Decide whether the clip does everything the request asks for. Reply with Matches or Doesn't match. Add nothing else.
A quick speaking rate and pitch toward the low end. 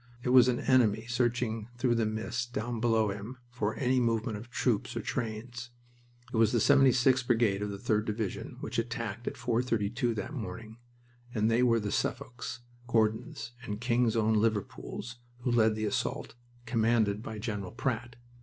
Doesn't match